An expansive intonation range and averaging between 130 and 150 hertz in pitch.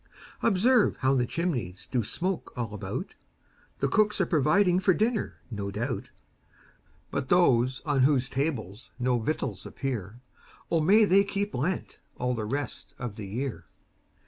Yes: wide, 7.1 semitones; low, 135 Hz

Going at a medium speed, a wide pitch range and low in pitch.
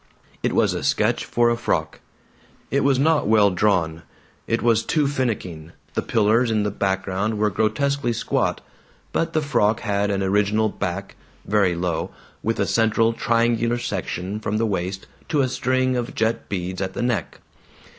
No: average, 165 wpm; average, 3.5 semitones; low, 110 Hz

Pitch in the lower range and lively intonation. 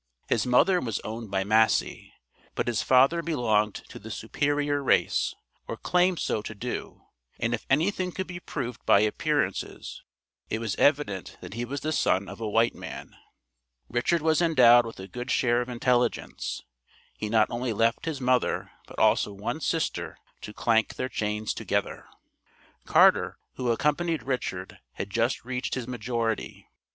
No: low, 120 Hz; average, 4.5 semitones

